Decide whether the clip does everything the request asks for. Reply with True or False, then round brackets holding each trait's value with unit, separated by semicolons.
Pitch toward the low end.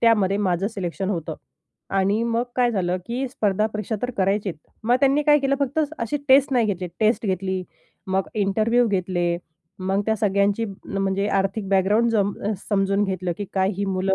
False (200 Hz)